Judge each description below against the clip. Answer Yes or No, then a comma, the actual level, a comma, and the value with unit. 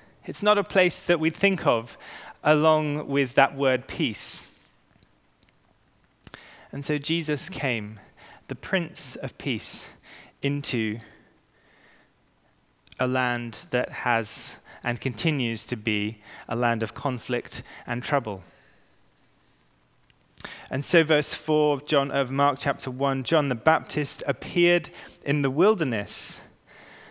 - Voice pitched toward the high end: No, medium, 140 Hz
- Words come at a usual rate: No, slow, 115 wpm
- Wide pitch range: No, average, 4.3 semitones